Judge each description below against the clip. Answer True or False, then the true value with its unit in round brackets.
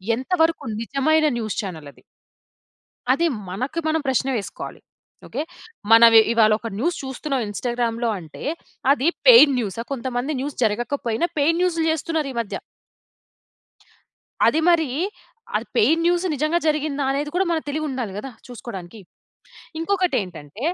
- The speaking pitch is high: True (270 Hz)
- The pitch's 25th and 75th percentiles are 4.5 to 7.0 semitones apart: True (5.6 semitones)